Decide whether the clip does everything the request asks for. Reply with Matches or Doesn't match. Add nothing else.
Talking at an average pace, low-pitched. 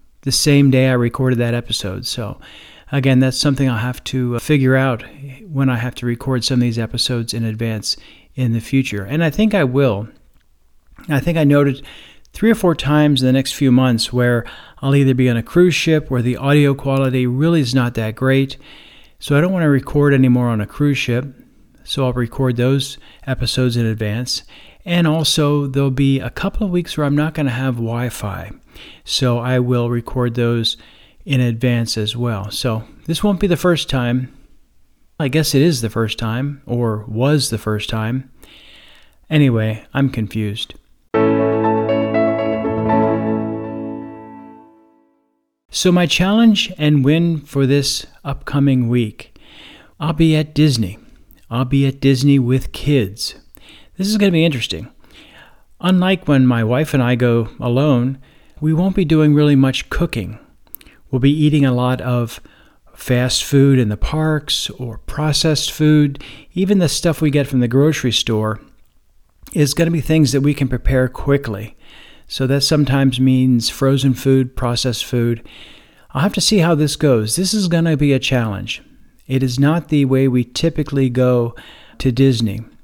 Matches